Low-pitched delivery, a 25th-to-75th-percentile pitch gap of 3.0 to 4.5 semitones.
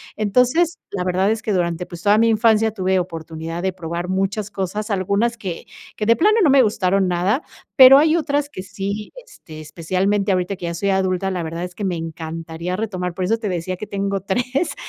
No: high, 195 Hz; average, 3.4 semitones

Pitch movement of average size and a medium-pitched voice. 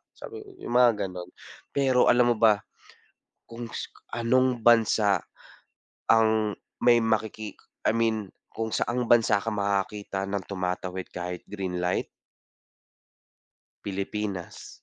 No: average, 3.2 semitones; low, 105 Hz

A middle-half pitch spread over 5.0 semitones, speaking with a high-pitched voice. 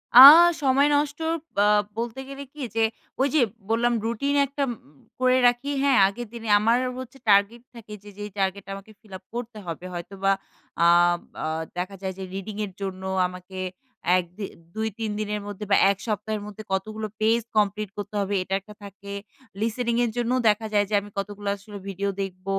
No: average, 3.2 semitones; high, 210 Hz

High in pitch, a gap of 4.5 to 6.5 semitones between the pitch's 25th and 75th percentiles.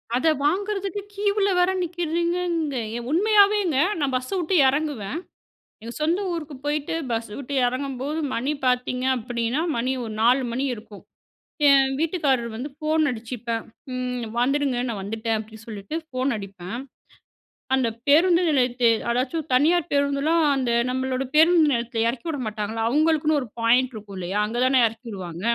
Yes: very high, 265 Hz; average, 5.2 semitones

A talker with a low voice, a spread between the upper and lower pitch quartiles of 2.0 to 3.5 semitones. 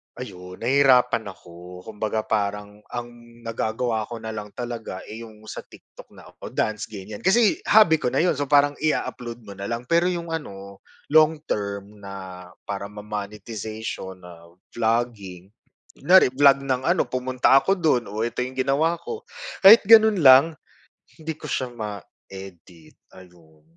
No: low, 115 Hz; wide, 5.5 semitones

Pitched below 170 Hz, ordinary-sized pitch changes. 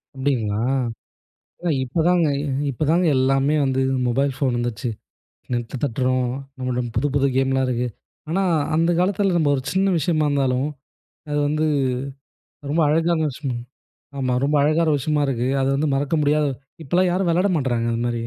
Yes: medium, 140 Hz; average, 3.9 semitones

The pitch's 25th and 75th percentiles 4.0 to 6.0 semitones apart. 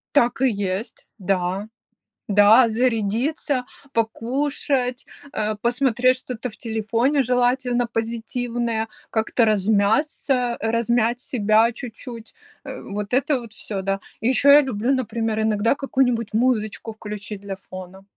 No: average, 2.8 semitones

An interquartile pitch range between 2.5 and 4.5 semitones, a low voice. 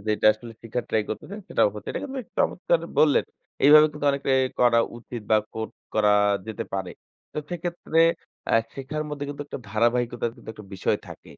No: wide, 5.5 semitones; low, 125 Hz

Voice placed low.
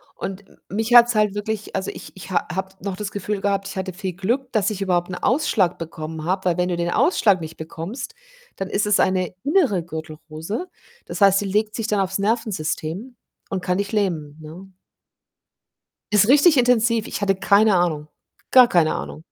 No: high, 195 Hz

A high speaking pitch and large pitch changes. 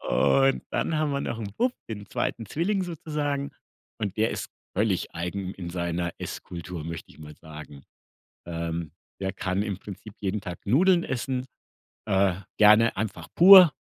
No: low, 105 Hz; wide, 8.0 semitones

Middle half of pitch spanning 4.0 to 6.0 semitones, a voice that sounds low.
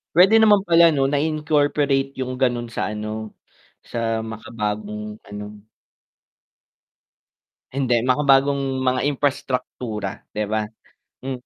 Yes: average, 4.6 semitones; low, 130 Hz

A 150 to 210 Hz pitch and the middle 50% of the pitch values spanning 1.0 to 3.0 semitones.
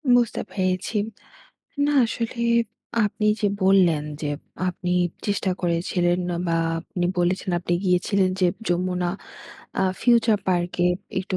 Yes: medium, 185 Hz; narrow, 2.4 semitones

